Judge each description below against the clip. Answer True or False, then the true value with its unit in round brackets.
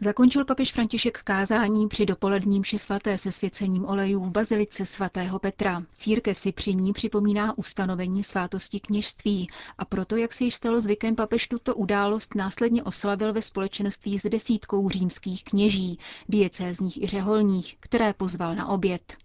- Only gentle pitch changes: True (2.0 semitones)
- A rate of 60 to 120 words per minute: False (145 wpm)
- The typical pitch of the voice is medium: False (200 Hz)